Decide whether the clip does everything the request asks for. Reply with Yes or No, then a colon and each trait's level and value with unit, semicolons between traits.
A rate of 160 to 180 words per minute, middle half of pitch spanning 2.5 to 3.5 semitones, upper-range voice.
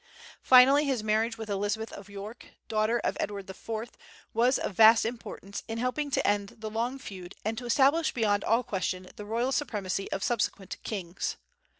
Yes: average, 175 wpm; average, 3.0 semitones; high, 220 Hz